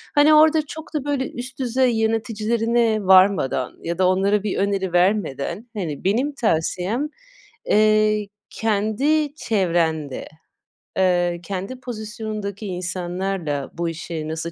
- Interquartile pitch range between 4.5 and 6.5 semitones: Yes, average, 4.9 semitones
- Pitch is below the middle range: No, high, 205 Hz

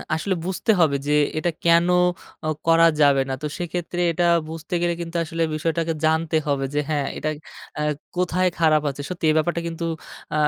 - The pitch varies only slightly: Yes, narrow, 2.0 semitones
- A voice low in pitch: No, medium, 165 Hz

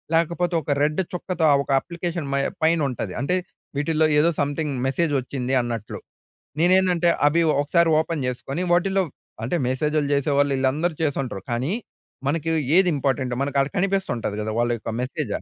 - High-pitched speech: No, medium, 150 Hz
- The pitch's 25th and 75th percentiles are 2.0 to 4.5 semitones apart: Yes, average, 4.2 semitones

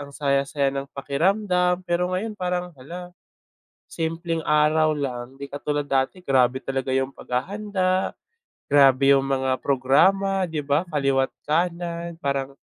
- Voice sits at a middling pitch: Yes, medium, 145 Hz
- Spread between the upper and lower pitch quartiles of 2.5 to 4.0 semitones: No, average, 4.5 semitones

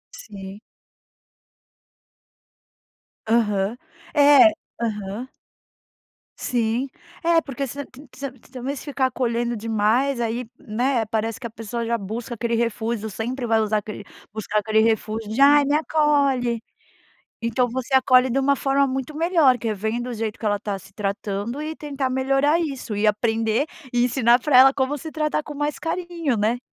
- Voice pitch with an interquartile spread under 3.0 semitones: No, average, 3.9 semitones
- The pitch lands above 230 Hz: Yes, high, 240 Hz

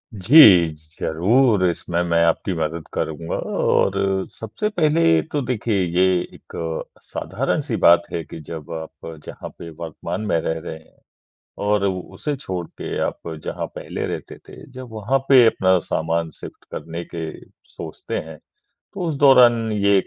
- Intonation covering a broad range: Yes, wide, 6.1 semitones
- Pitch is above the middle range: No, very low, 95 Hz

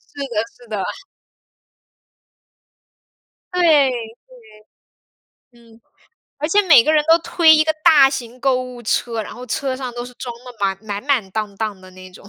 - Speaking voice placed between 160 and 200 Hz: No, high, 245 Hz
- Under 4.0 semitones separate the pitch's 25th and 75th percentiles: No, average, 4.3 semitones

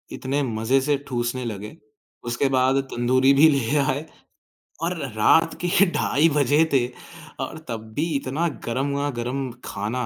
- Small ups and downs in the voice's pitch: No, average, 3.1 semitones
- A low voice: Yes, low, 130 Hz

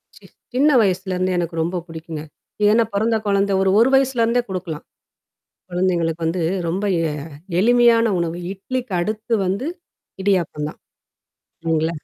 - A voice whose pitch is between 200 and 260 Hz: No, high, 190 Hz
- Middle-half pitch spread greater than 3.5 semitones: Yes, average, 5.1 semitones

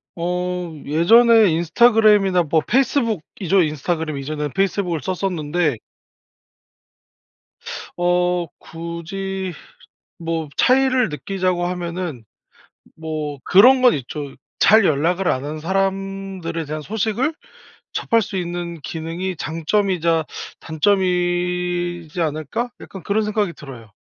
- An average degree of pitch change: Yes, average, 3.4 semitones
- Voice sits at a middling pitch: Yes, medium, 175 Hz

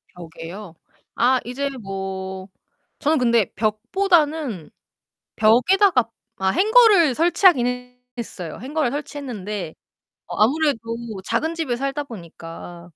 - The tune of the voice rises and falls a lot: Yes, wide, 7.6 semitones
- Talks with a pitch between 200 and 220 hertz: No, high, 245 Hz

